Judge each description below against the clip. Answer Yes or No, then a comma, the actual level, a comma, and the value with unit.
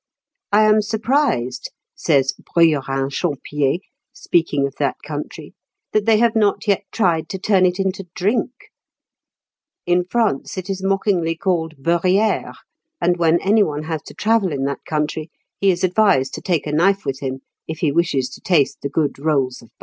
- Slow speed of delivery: No, average, 175 wpm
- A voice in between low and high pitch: Yes, medium, 170 Hz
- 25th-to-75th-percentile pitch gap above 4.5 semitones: Yes, average, 5.2 semitones